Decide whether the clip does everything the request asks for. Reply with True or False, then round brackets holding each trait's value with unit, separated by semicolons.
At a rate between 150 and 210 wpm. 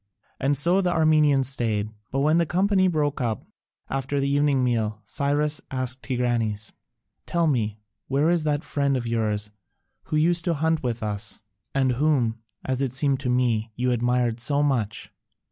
True (165 wpm)